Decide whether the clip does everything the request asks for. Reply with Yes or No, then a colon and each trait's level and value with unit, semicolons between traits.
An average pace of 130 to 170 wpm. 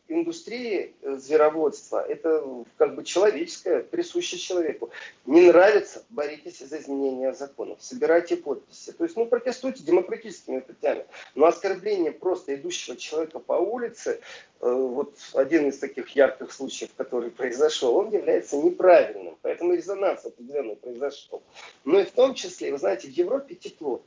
Yes: average, 135 wpm